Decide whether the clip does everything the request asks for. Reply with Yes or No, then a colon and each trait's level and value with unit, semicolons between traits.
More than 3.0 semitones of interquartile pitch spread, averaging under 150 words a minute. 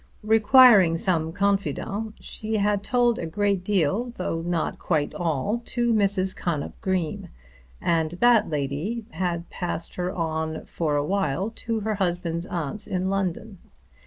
Yes: average, 4.3 semitones; average, 140 wpm